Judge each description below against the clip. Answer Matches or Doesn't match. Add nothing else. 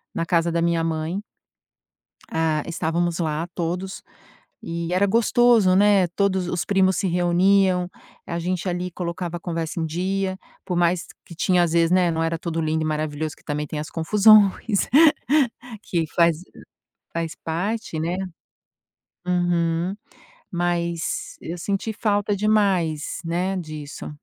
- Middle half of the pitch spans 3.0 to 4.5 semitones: Doesn't match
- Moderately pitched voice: Matches